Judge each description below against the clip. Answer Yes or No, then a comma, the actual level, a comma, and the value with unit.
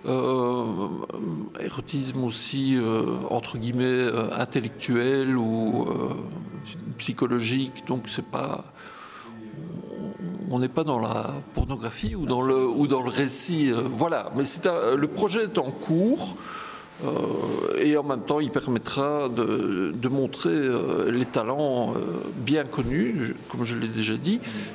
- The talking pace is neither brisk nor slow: No, slow, 140 wpm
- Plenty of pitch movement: No, average, 3.7 semitones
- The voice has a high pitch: No, low, 130 Hz